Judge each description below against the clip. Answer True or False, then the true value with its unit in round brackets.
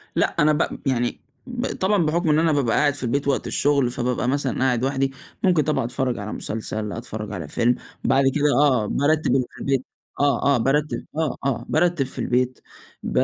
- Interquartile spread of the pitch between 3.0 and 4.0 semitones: True (3.5 semitones)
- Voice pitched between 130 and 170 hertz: True (135 Hz)